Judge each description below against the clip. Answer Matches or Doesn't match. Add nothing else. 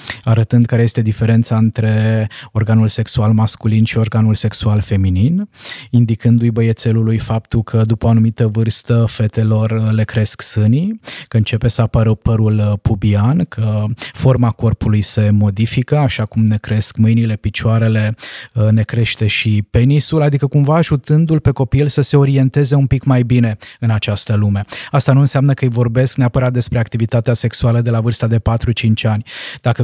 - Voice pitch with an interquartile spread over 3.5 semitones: Doesn't match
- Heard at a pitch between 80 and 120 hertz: Matches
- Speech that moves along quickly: Doesn't match